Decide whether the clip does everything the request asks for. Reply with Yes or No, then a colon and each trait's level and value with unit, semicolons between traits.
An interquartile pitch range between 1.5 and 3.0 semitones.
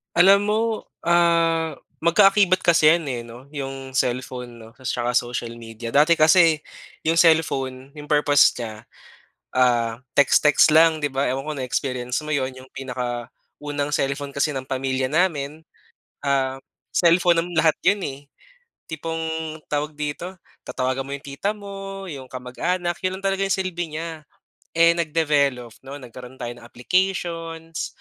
No: average, 4.3 semitones